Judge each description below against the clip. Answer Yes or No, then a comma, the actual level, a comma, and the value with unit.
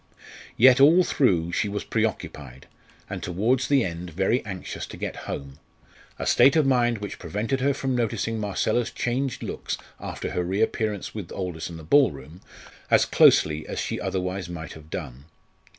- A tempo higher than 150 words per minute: Yes, average, 165 wpm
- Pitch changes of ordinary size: No, wide, 6.5 semitones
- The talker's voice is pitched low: Yes, low, 100 Hz